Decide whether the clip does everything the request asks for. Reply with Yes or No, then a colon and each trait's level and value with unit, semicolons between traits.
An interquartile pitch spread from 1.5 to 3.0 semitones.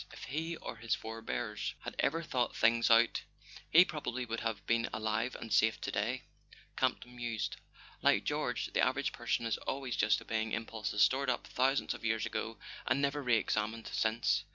Yes: narrow, 2.4 semitones